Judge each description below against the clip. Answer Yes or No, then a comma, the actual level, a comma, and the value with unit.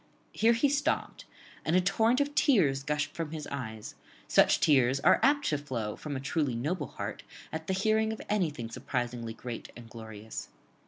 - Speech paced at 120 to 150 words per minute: No, average, 175 wpm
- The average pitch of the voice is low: No, medium, 150 Hz